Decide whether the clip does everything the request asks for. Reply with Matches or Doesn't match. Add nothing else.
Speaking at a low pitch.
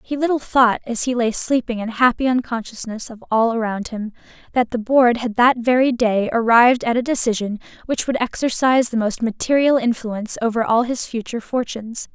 Doesn't match